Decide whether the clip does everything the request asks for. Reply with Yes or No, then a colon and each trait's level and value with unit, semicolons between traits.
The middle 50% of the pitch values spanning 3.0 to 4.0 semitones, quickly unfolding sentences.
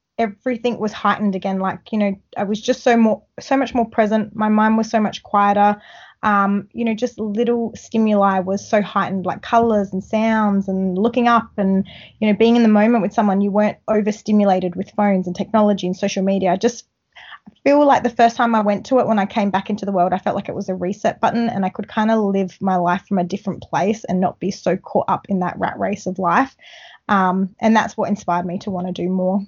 No: narrow, 2.6 semitones; fast, 240 wpm